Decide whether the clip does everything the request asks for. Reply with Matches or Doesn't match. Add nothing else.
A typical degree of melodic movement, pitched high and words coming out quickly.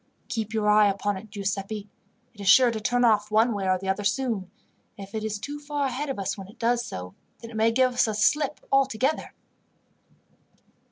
Matches